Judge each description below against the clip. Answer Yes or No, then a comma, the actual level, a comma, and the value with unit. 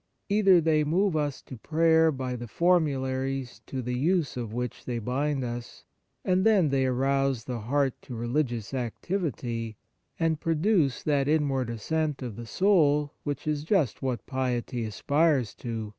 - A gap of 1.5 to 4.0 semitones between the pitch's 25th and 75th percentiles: No, average, 4.4 semitones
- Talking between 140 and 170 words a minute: Yes, average, 160 wpm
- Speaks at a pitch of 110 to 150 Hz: Yes, low, 135 Hz